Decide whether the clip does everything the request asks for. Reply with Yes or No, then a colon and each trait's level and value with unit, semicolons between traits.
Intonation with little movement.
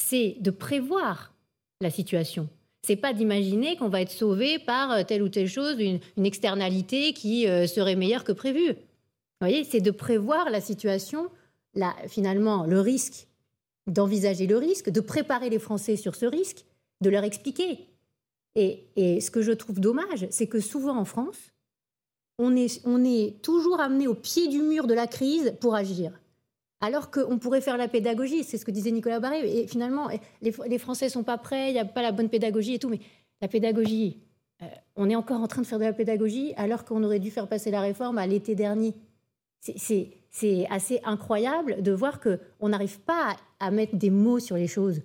No: average, 3.8 semitones